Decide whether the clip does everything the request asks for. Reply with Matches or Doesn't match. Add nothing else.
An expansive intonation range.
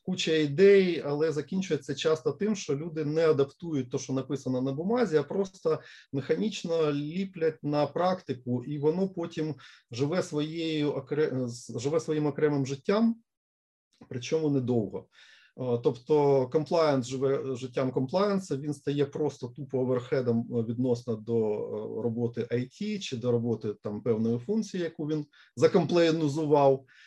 Doesn't match